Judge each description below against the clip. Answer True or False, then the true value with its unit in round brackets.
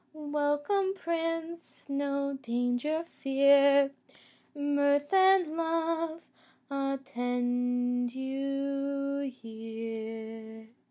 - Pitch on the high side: True (280 Hz)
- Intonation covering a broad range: False (3.7 semitones)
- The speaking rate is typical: False (60 wpm)